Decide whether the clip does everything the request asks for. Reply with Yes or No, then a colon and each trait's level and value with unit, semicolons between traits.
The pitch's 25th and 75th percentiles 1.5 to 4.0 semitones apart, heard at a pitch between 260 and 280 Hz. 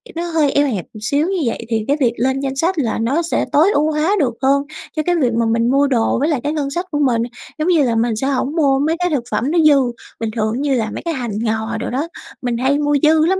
No: average, 4.7 semitones; very high, 275 Hz